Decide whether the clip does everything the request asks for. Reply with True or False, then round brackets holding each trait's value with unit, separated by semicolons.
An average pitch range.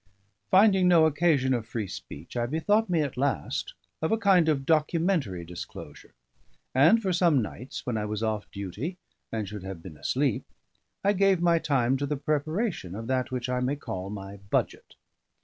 False (7.8 semitones)